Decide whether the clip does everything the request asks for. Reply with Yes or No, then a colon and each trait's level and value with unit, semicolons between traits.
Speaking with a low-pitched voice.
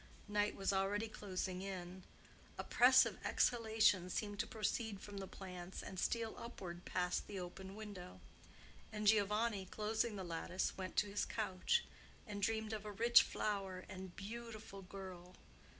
No: high, 200 Hz